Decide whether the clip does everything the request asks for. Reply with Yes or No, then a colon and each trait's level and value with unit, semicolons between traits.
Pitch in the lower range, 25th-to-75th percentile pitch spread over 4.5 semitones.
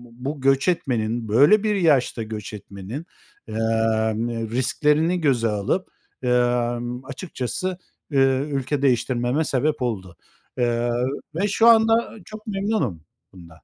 Yes: low, 130 Hz; average, 5.2 semitones